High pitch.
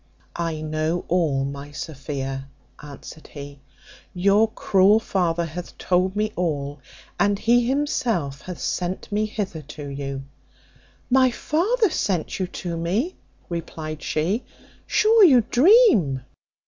No: medium, 175 Hz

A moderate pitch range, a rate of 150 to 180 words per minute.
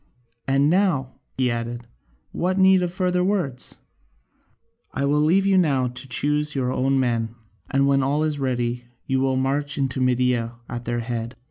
Yes: average, 3.3 semitones; average, 165 wpm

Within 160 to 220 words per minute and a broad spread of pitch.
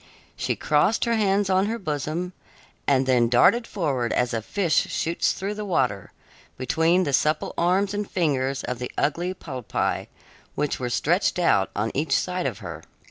Yes: average, 170 wpm; wide, 6.4 semitones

